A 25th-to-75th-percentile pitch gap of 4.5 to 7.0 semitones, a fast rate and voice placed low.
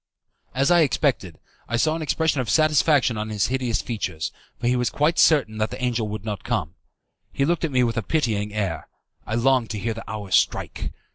Yes: average, 4.8 semitones; fast, 215 wpm; low, 120 Hz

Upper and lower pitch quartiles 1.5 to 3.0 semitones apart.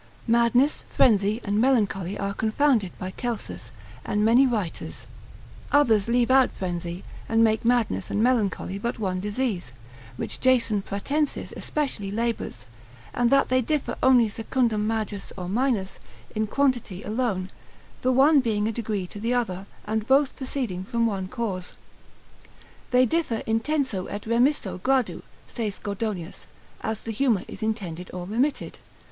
No: average, 4.1 semitones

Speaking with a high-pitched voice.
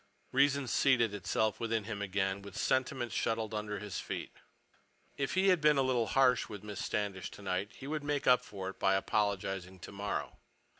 No: low, 105 Hz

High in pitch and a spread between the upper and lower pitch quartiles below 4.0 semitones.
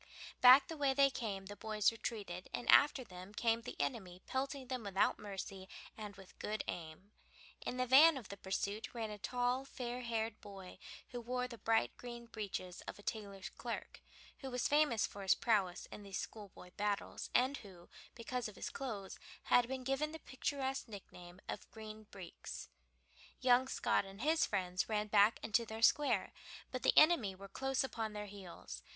No: high, 220 Hz; average, 4.3 semitones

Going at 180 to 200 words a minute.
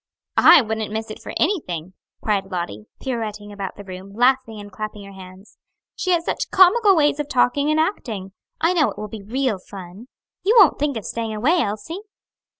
Yes: average, 190 wpm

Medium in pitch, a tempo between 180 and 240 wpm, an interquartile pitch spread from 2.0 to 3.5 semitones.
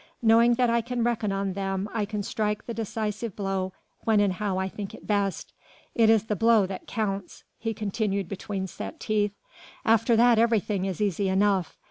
No: high, 210 Hz; average, 185 wpm; narrow, 2.5 semitones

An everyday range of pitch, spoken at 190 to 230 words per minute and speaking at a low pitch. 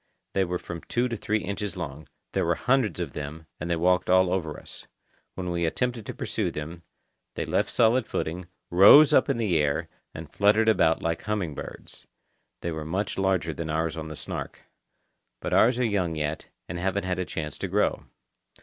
Yes: average, 4.2 semitones; average, 195 wpm; very low, 90 Hz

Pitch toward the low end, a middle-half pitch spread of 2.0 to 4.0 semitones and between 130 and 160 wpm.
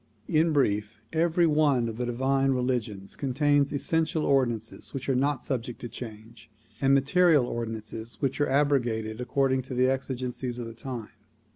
Yes: low, 130 Hz; average, 3.2 semitones; average, 150 wpm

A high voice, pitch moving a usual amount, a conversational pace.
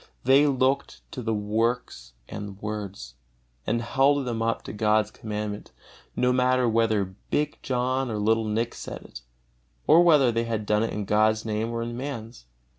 No: low, 115 Hz; average, 3.0 semitones; average, 170 wpm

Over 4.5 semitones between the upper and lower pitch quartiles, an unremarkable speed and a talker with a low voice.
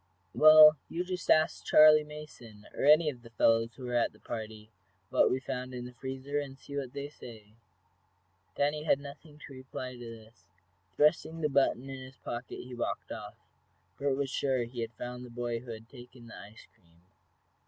No: average, 3.5 semitones; average, 195 wpm; low, 130 Hz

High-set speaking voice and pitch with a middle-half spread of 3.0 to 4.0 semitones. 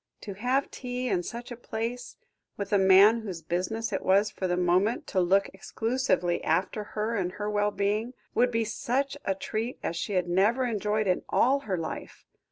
Yes: high, 210 Hz; average, 3.7 semitones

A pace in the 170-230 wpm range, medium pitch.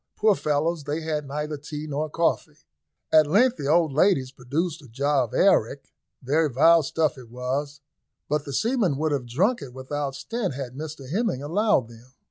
Yes: average, 180 wpm; medium, 150 Hz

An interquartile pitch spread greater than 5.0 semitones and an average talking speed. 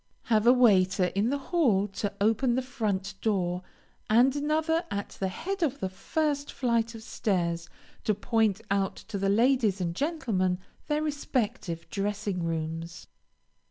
Yes: wide, 5.6 semitones; average, 150 wpm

